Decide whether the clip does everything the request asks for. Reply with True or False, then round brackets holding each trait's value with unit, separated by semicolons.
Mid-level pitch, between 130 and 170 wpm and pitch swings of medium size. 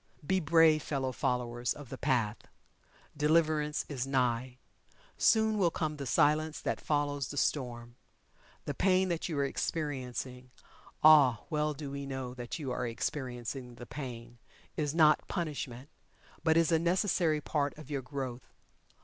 True (145 Hz; 150 wpm; 3.7 semitones)